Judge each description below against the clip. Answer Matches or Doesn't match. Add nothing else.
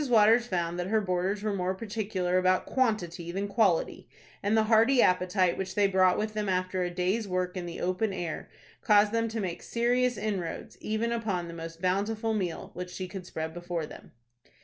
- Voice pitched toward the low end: Doesn't match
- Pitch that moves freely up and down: Doesn't match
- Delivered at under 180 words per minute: Doesn't match